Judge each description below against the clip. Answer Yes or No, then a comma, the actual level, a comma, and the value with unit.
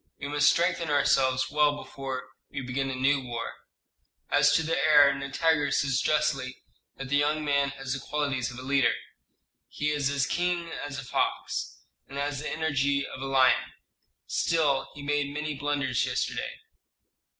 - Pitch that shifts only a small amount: Yes, narrow, 1.8 semitones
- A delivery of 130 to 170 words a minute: Yes, average, 165 wpm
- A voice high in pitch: No, medium, 140 Hz